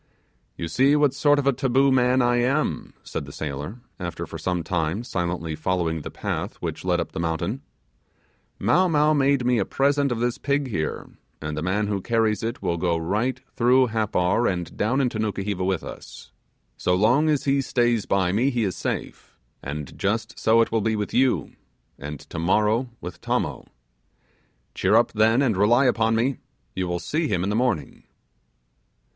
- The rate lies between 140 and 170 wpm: No, average, 185 wpm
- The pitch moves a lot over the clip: Yes, wide, 6.1 semitones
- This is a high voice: No, low, 110 Hz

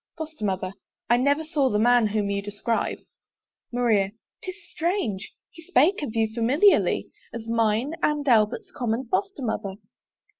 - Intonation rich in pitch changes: Yes, wide, 5.9 semitones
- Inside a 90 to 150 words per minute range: Yes, average, 145 wpm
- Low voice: No, high, 240 Hz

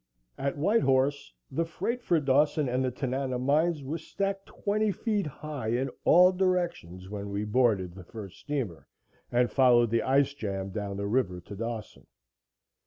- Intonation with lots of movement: Yes, wide, 6.6 semitones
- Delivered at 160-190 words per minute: Yes, average, 165 wpm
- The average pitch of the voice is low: Yes, low, 130 Hz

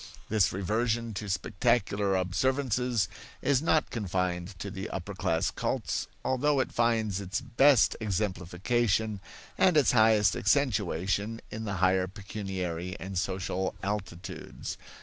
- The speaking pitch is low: Yes, low, 100 Hz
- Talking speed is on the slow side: Yes, slow, 120 wpm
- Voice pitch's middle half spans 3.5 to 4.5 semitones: Yes, average, 3.8 semitones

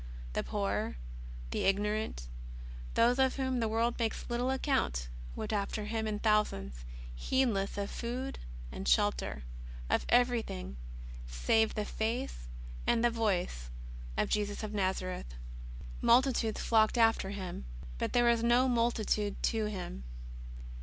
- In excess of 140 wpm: No, slow, 135 wpm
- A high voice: Yes, high, 215 Hz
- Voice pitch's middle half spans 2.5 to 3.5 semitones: No, average, 3.9 semitones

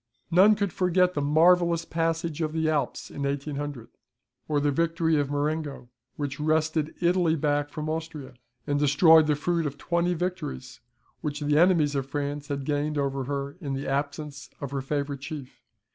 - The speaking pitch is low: No, medium, 150 Hz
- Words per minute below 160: No, average, 170 wpm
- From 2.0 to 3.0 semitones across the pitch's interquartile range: Yes, narrow, 2.4 semitones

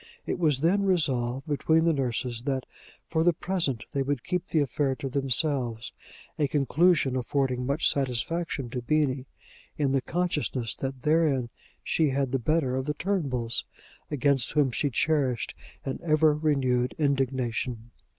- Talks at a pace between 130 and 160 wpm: Yes, average, 150 wpm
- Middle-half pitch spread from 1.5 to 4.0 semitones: Yes, average, 3.4 semitones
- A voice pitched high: No, medium, 140 Hz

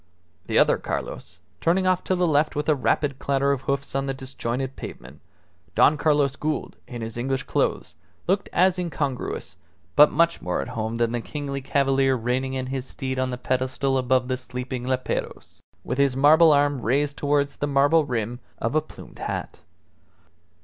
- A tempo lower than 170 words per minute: No, average, 175 wpm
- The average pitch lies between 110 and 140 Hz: Yes, low, 135 Hz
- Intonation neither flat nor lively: No, narrow, 2.3 semitones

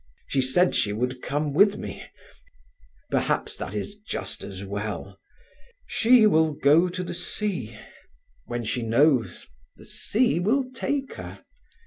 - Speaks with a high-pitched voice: No, medium, 150 Hz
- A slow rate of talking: Yes, slow, 130 wpm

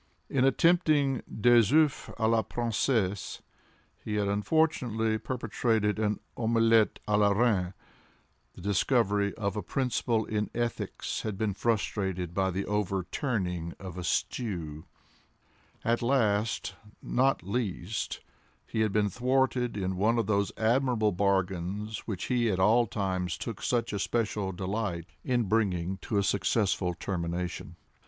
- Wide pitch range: No, average, 3.5 semitones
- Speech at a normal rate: No, slow, 130 wpm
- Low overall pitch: Yes, low, 105 Hz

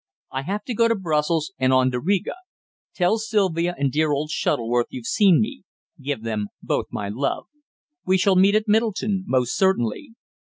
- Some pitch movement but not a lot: No, wide, 7.7 semitones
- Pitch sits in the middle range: Yes, medium, 170 Hz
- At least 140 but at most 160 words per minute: No, average, 185 wpm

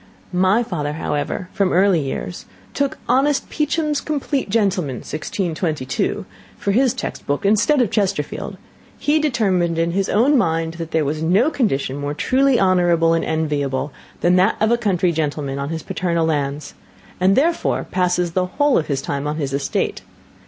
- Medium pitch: Yes, medium, 180 Hz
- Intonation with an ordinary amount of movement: No, wide, 6.4 semitones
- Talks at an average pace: Yes, average, 150 wpm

